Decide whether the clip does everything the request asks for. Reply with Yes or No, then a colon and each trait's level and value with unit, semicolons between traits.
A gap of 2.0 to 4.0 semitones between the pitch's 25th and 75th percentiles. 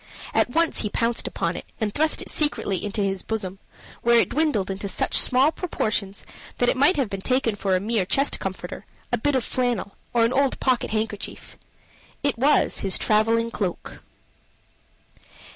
No: average, 4.6 semitones